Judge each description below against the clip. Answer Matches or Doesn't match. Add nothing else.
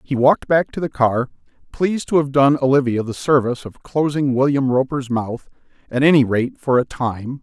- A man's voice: Matches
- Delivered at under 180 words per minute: Doesn't match